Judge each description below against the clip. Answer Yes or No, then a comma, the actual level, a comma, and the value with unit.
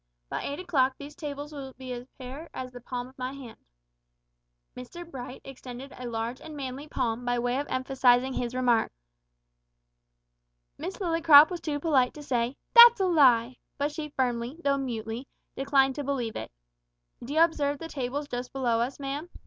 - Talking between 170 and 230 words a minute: Yes, average, 175 wpm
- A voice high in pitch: Yes, very high, 265 Hz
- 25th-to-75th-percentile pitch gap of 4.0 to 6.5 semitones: No, average, 2.9 semitones